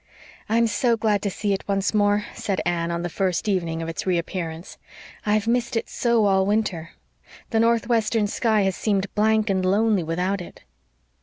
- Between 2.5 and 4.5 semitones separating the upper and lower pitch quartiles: Yes, average, 3.2 semitones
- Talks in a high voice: Yes, high, 200 Hz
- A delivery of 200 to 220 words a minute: No, average, 175 wpm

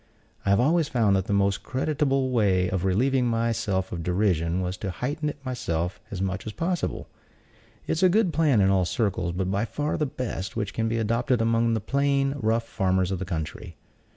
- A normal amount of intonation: No, wide, 5.8 semitones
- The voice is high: No, low, 110 Hz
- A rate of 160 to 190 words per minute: No, fast, 205 wpm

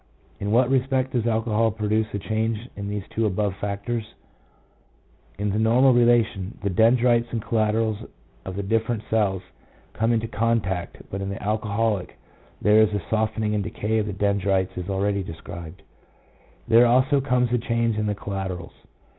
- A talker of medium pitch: No, low, 110 Hz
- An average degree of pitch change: No, narrow, 2.3 semitones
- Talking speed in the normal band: Yes, average, 165 wpm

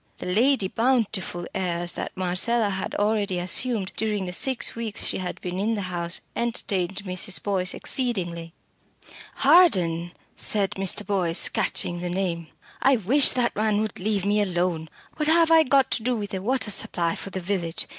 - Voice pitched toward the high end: Yes, high, 195 Hz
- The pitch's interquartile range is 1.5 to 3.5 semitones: No, average, 4.3 semitones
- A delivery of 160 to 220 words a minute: Yes, average, 170 wpm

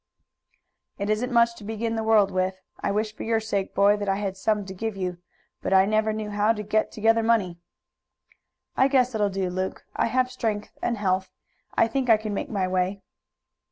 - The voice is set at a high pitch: Yes, high, 210 Hz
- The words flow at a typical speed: No, fast, 210 wpm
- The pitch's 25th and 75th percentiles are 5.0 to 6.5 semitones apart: No, narrow, 2.5 semitones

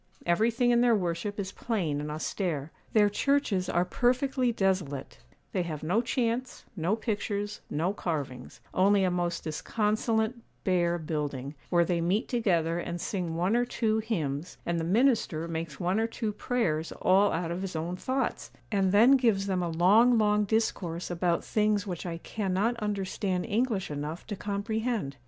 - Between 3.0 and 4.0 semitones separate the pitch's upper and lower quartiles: No, average, 4.5 semitones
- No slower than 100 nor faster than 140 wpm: No, average, 165 wpm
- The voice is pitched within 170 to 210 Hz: Yes, high, 190 Hz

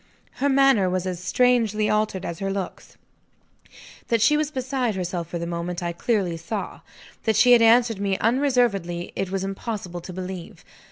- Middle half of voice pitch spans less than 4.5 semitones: No, average, 4.9 semitones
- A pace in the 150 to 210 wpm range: Yes, average, 170 wpm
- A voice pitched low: No, high, 200 Hz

